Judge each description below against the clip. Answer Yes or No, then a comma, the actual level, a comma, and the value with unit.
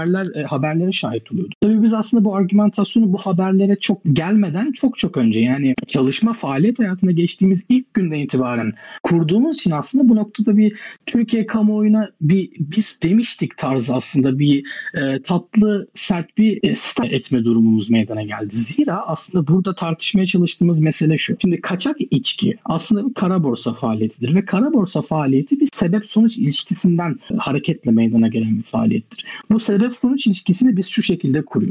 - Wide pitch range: Yes, wide, 6.8 semitones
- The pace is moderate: No, fast, 155 wpm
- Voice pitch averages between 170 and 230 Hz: Yes, high, 190 Hz